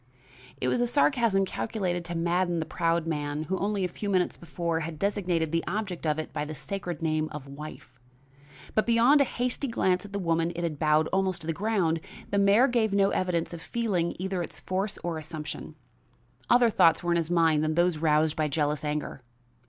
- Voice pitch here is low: No, medium, 170 Hz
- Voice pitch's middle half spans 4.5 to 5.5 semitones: No, average, 4.0 semitones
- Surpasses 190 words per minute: Yes, fast, 205 wpm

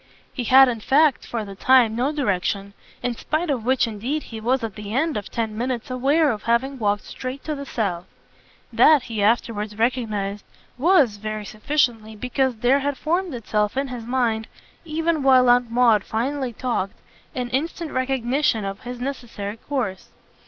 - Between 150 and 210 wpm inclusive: Yes, average, 170 wpm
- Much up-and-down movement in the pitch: No, average, 3.9 semitones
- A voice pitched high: Yes, high, 245 Hz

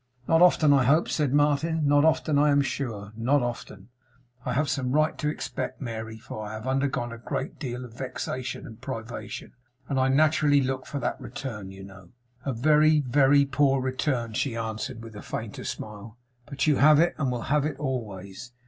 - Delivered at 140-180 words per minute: No, average, 195 wpm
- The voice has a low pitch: Yes, low, 130 Hz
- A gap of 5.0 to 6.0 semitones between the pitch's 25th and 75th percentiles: No, average, 4.1 semitones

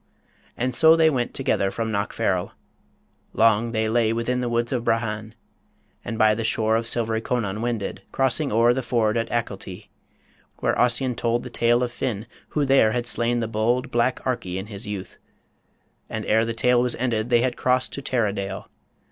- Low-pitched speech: Yes, low, 115 Hz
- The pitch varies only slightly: Yes, narrow, 2.1 semitones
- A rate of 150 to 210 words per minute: Yes, average, 180 wpm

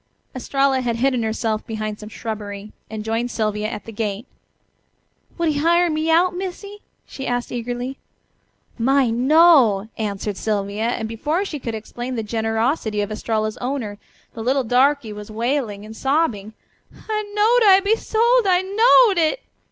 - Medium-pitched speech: No, high, 245 Hz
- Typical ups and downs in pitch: No, wide, 6.6 semitones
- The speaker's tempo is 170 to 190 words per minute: No, average, 155 wpm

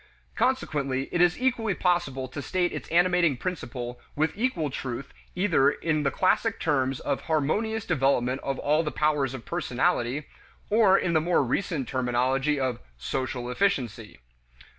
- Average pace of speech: Yes, average, 145 wpm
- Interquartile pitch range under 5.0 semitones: No, average, 5.3 semitones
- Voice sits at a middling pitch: Yes, medium, 150 Hz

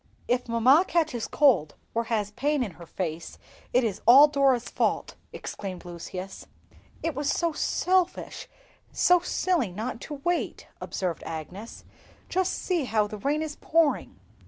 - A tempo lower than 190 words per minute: Yes, average, 140 wpm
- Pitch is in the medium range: No, very high, 250 Hz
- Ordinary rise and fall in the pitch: No, wide, 7.0 semitones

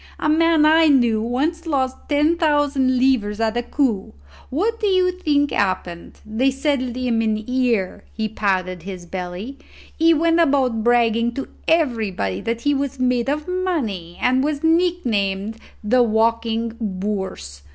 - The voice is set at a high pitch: Yes, very high, 250 Hz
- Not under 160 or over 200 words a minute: No, average, 150 wpm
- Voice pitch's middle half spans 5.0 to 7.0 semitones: Yes, wide, 5.5 semitones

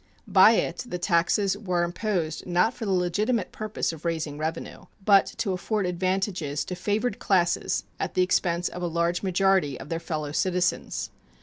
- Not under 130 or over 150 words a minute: No, average, 170 wpm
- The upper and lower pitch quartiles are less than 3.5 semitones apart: Yes, narrow, 2.5 semitones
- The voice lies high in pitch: No, medium, 180 Hz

